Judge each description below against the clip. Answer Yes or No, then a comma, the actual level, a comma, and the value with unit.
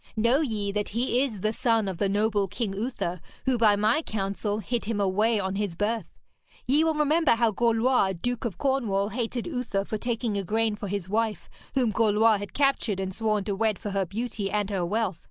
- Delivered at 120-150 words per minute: No, average, 200 wpm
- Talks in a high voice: Yes, high, 215 Hz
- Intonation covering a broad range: No, average, 2.9 semitones